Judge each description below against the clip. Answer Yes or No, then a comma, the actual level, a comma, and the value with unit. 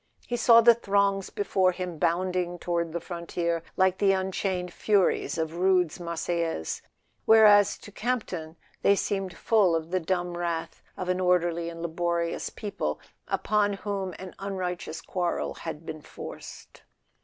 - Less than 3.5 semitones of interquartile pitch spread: Yes, narrow, 2.5 semitones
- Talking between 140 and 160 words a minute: Yes, average, 150 wpm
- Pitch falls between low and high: Yes, medium, 180 Hz